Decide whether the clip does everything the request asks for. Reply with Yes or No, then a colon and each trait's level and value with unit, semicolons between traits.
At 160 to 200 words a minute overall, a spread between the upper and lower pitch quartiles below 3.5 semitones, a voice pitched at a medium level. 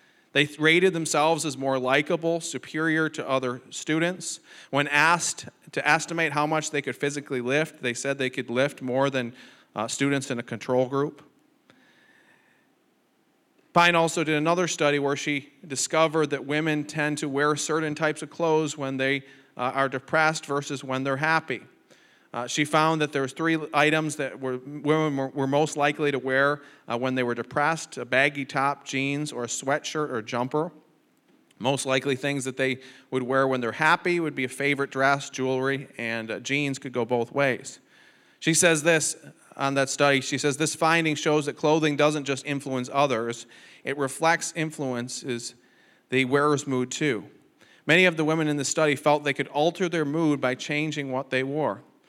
Yes: average, 180 wpm; average, 2.8 semitones; medium, 145 Hz